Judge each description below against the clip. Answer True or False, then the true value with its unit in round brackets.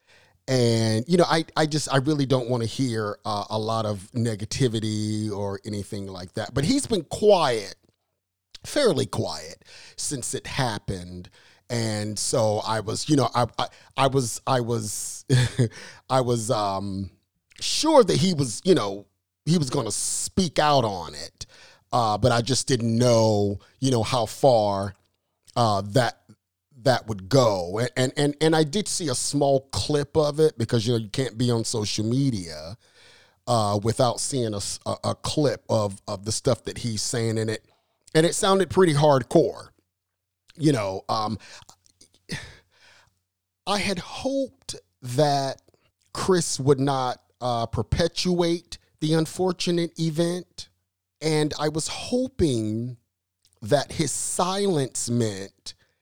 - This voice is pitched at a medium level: False (120 Hz)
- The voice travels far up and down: True (6.1 semitones)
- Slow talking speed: False (150 wpm)